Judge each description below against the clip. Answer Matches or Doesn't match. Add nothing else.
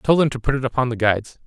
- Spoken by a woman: Doesn't match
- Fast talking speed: Matches